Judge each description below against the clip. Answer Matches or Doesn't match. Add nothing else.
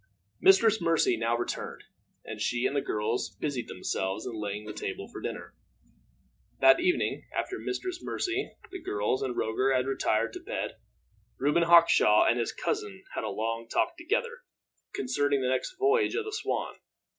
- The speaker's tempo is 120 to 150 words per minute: Doesn't match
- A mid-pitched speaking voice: Matches